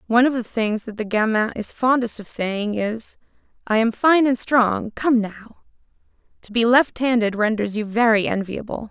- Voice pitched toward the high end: Yes, high, 225 Hz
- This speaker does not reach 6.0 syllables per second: Yes, 4.7 syllables/s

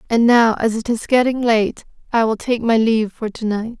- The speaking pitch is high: Yes, high, 225 Hz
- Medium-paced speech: No, fast, 235 wpm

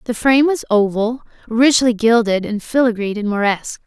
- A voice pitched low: No, high, 230 Hz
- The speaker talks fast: No, average, 155 wpm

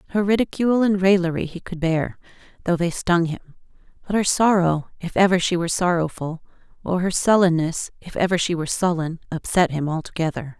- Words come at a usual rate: Yes, average, 170 wpm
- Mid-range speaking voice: Yes, medium, 175 Hz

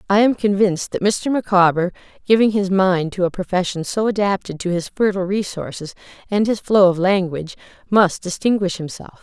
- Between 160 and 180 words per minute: Yes, average, 170 wpm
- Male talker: No, female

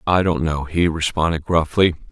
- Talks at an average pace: Yes, average, 170 wpm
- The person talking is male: Yes, male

